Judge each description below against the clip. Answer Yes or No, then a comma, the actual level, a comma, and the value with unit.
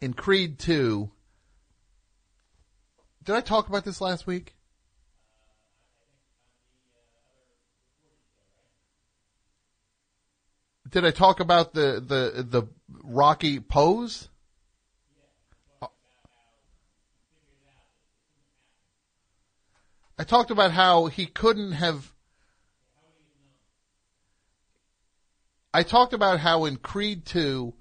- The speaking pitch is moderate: No, low, 125 Hz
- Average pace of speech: No, slow, 70 wpm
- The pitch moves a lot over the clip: Yes, wide, 8.8 semitones